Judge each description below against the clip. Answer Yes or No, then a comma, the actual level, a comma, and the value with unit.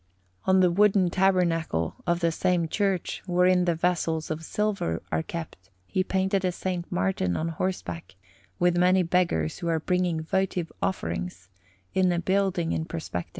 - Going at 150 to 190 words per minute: Yes, average, 155 wpm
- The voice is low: No, medium, 175 Hz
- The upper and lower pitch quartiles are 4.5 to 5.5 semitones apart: No, narrow, 2.6 semitones